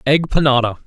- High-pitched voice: No, low, 135 Hz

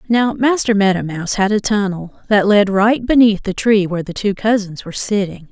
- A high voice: Yes, high, 205 Hz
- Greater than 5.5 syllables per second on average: No, 5.4 syllables/s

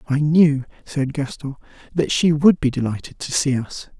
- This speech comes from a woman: No, male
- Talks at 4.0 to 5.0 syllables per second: Yes, 4.6 syllables/s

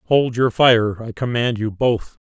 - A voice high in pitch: No, low, 115 Hz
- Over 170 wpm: No, average, 160 wpm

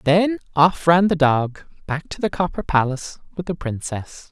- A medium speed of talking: Yes, average, 180 wpm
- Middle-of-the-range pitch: Yes, medium, 155 Hz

